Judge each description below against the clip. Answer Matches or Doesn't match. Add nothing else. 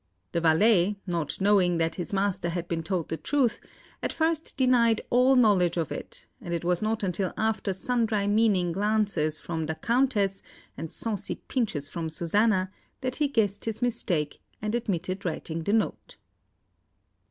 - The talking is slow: Doesn't match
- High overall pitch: Matches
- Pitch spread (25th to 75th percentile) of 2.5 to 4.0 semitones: Doesn't match